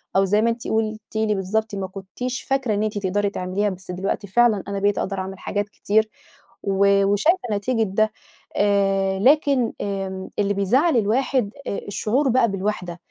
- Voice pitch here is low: No, high, 205 Hz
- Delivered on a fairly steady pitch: Yes, narrow, 2.3 semitones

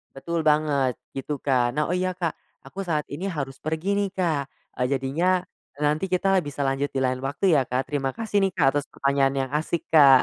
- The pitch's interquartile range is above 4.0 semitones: Yes, average, 4.7 semitones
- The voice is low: No, medium, 150 Hz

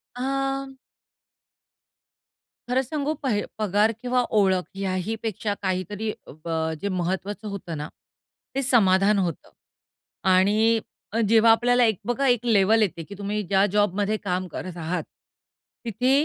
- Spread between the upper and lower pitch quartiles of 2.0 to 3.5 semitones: No, average, 4.1 semitones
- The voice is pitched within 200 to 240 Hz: Yes, high, 210 Hz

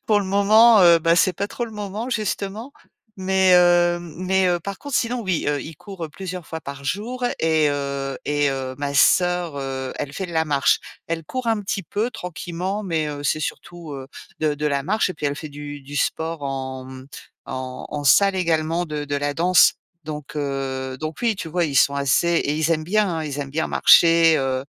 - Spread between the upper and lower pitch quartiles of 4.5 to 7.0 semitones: Yes, average, 4.9 semitones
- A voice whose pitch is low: No, medium, 165 Hz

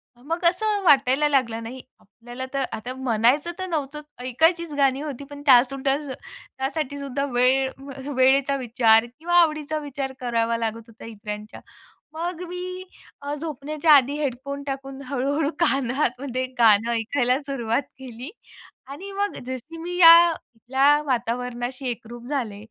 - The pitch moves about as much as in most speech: Yes, average, 3.5 semitones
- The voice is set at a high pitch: Yes, very high, 270 Hz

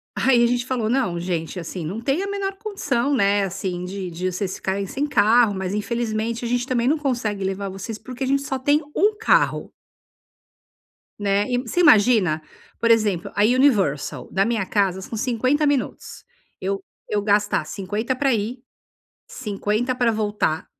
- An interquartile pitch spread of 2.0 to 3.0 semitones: No, average, 4.7 semitones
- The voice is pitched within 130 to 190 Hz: No, high, 220 Hz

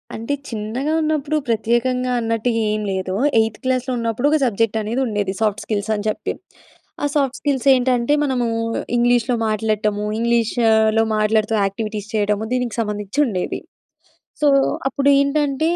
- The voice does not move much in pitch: No, average, 3.2 semitones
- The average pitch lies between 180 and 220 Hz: No, high, 230 Hz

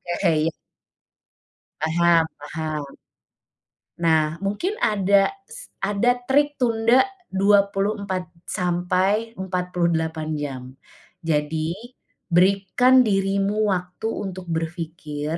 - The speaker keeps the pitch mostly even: No, average, 3.9 semitones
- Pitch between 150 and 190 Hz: Yes, medium, 185 Hz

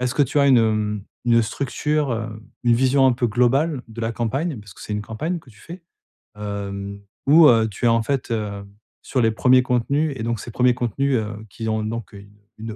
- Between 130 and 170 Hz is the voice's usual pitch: No, low, 115 Hz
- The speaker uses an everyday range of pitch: Yes, average, 3.7 semitones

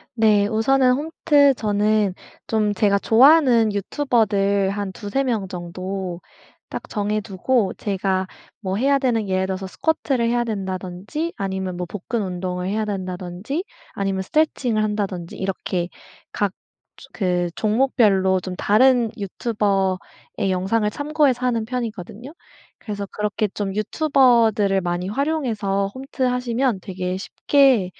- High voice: Yes, high, 210 Hz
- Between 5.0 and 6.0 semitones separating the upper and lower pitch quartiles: No, average, 4.2 semitones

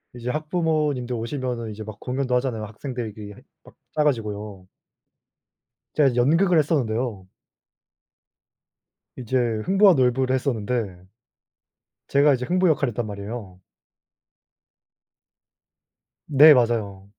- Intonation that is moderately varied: Yes, average, 4.8 semitones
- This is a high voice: No, low, 125 Hz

